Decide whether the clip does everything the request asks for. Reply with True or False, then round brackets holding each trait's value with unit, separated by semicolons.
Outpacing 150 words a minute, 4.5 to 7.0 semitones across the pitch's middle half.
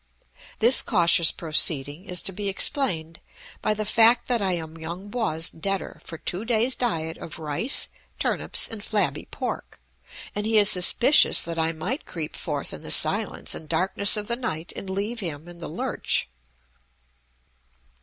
True (165 wpm; 5.1 semitones)